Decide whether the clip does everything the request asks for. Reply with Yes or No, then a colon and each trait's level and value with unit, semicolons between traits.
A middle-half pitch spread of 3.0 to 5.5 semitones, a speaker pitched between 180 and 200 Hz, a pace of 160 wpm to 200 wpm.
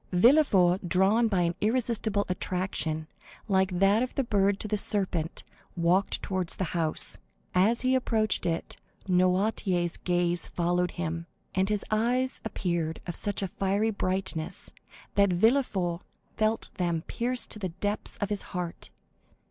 No: average, 3.4 semitones; high, 190 Hz; average, 140 wpm